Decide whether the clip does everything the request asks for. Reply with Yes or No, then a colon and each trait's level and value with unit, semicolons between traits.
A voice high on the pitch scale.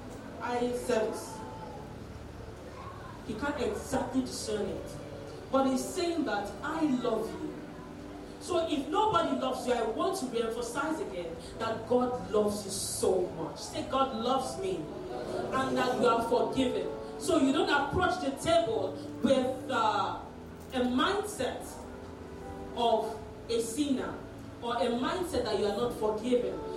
Yes: very high, 255 Hz